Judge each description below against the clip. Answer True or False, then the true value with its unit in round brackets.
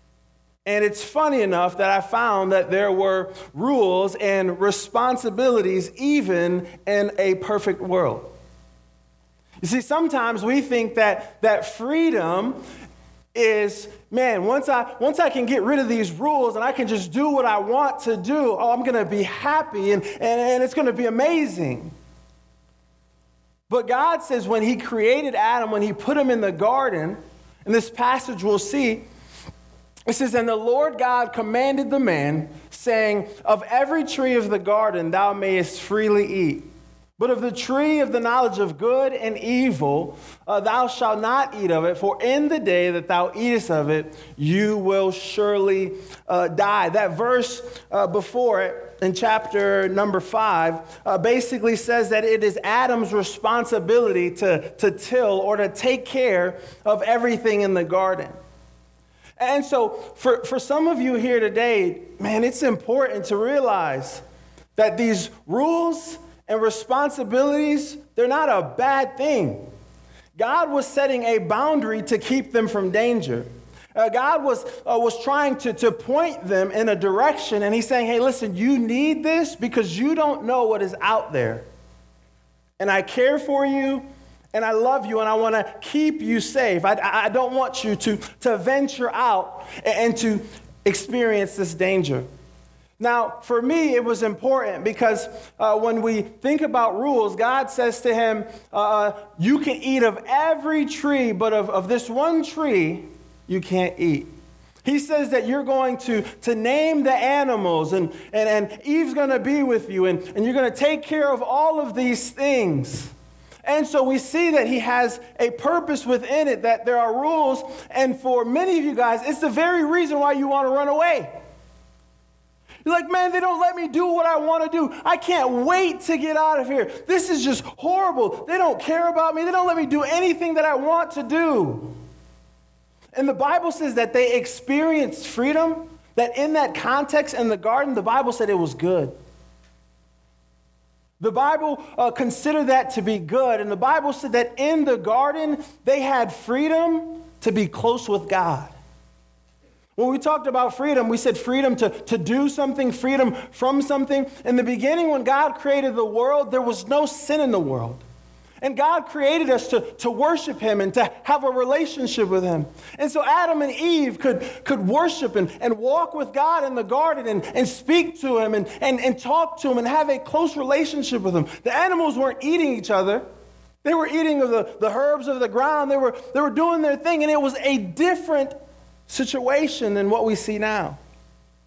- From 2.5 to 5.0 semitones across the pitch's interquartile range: False (5.6 semitones)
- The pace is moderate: True (180 wpm)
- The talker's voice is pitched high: True (245 Hz)